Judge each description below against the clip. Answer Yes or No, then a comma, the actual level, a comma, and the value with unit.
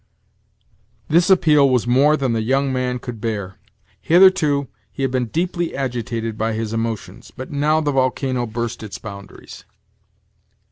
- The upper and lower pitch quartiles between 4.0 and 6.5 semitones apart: Yes, average, 4.3 semitones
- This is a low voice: Yes, low, 130 Hz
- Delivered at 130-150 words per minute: Yes, average, 145 wpm